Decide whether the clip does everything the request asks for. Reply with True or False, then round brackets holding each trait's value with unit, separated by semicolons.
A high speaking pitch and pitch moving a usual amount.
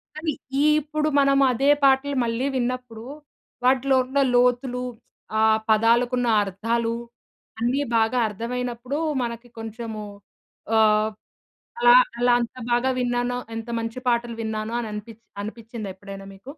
False (240 Hz; 2.3 semitones)